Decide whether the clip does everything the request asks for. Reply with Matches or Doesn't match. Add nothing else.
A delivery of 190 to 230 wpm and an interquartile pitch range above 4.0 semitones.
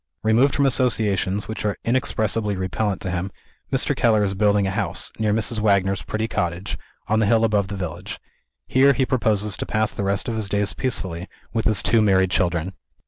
Doesn't match